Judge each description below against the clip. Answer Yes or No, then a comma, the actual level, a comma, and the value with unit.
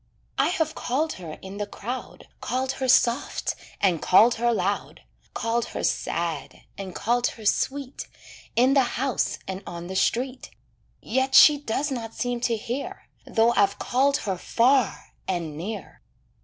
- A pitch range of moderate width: Yes, average, 4.9 semitones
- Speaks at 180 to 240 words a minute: No, average, 155 wpm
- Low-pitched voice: No, high, 235 Hz